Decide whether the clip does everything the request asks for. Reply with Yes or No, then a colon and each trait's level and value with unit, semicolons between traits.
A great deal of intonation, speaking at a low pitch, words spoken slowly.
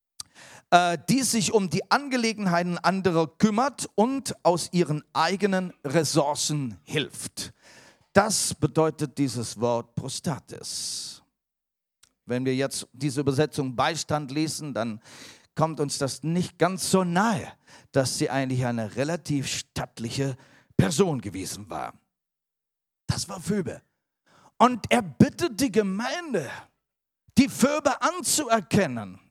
No: wide, 6.1 semitones; medium, 155 Hz; slow, 110 wpm